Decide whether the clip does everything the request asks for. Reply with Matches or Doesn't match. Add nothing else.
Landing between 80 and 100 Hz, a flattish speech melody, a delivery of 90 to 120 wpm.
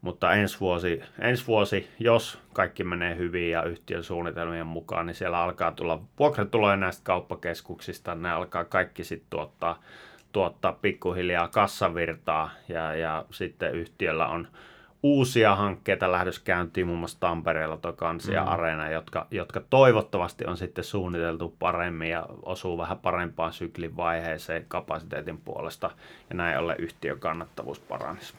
Doesn't match